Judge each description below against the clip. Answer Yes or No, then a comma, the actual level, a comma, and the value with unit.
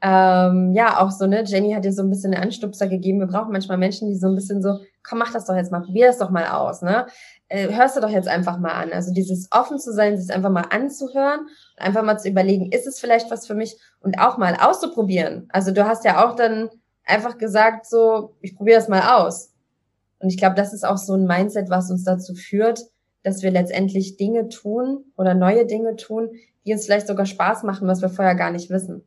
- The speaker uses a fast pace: Yes, fast, 235 wpm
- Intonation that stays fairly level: No, average, 3.1 semitones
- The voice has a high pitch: Yes, high, 200 Hz